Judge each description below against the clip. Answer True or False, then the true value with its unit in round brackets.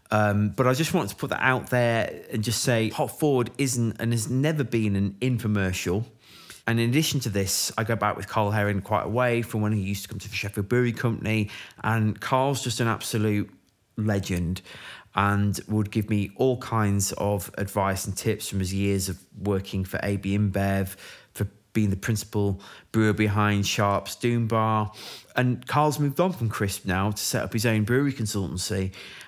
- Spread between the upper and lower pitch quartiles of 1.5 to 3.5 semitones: True (2.8 semitones)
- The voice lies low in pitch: True (105 Hz)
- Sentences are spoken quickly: False (195 wpm)